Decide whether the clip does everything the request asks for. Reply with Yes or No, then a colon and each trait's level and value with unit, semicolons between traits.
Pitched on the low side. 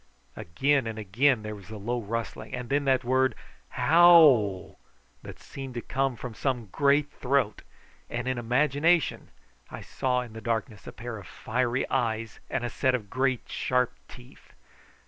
Yes: low, 125 Hz